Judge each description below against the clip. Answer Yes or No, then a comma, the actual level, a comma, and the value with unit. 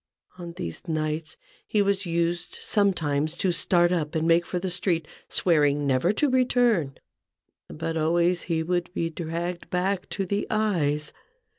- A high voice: No, medium, 170 Hz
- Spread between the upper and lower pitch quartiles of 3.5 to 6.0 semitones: No, average, 2.7 semitones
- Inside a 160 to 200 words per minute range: No, average, 150 wpm